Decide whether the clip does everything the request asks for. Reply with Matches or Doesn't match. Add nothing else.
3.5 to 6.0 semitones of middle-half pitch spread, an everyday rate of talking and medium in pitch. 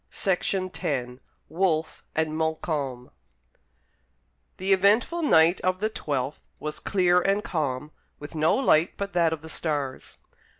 Doesn't match